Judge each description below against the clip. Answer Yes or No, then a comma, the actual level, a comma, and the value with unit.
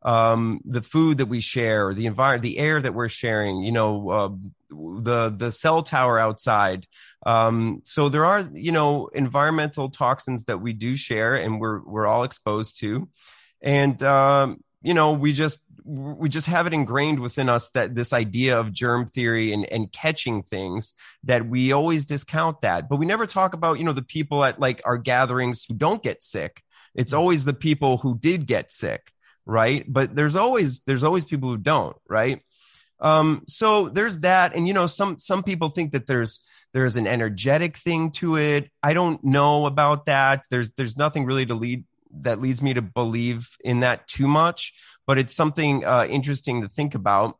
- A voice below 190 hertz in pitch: Yes, low, 135 Hz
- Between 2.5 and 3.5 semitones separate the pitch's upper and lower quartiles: No, average, 4.4 semitones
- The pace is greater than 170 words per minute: Yes, average, 190 wpm